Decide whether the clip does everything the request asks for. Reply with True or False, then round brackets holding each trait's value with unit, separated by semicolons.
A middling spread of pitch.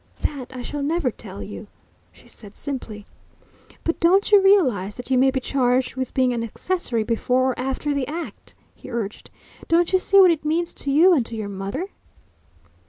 False (6.0 semitones)